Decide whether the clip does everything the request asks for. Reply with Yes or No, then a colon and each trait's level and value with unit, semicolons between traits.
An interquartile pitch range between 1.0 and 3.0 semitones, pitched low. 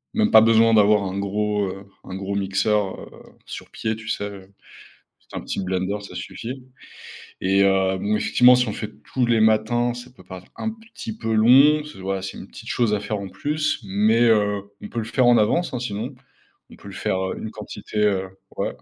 No: average, 3.5 semitones; low, 105 Hz